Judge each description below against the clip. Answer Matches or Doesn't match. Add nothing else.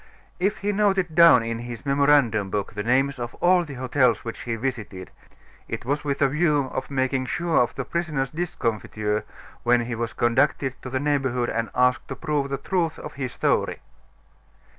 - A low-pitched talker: Matches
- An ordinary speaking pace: Matches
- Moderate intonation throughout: Matches